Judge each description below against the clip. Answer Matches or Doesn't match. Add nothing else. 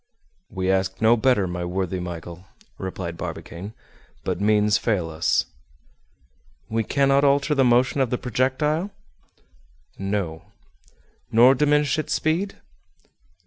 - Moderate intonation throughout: Doesn't match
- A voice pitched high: Doesn't match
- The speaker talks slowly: Matches